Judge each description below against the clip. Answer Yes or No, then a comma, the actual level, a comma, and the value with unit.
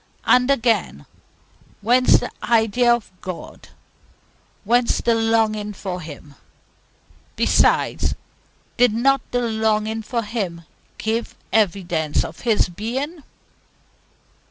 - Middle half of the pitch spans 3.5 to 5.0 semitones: No, average, 3.1 semitones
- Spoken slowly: Yes, slow, 100 wpm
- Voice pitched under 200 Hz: No, high, 220 Hz